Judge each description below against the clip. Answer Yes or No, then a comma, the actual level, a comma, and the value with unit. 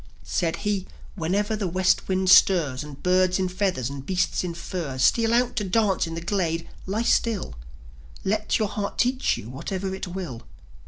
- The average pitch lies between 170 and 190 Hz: Yes, medium, 185 Hz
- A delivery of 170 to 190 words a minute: Yes, average, 175 wpm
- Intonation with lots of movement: No, average, 3.7 semitones